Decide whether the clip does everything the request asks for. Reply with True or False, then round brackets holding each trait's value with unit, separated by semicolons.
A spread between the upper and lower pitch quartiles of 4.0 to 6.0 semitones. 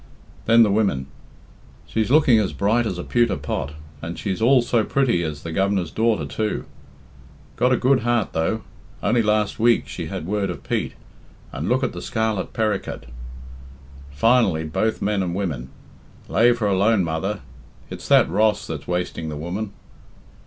True (4.6 semitones)